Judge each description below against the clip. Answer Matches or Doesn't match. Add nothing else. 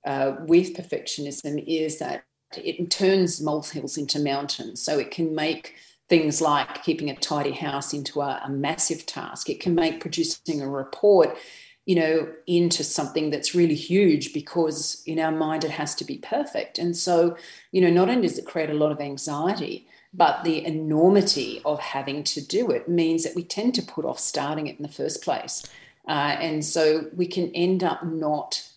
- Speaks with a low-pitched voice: Doesn't match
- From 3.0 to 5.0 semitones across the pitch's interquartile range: Doesn't match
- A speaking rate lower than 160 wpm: Doesn't match